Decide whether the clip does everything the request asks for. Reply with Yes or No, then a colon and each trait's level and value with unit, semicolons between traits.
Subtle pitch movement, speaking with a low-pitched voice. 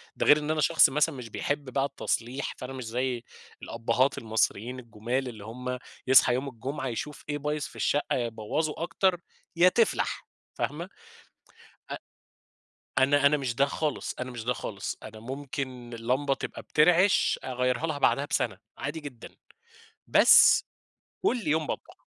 No: average, 3.5 semitones; low, 130 Hz